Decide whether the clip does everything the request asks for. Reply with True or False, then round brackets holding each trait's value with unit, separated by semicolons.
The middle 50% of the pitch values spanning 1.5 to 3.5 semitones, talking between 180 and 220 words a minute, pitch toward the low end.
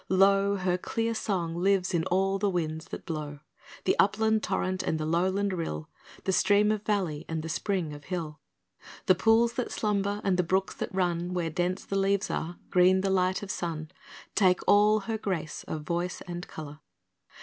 False (3.0 semitones; 185 wpm; 185 Hz)